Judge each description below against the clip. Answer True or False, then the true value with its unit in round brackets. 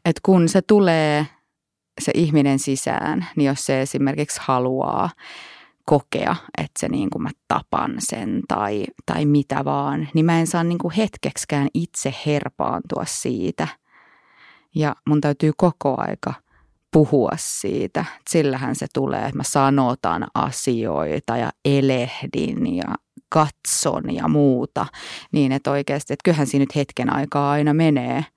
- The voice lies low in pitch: False (145 Hz)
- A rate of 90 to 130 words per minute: False (140 wpm)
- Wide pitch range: False (2.5 semitones)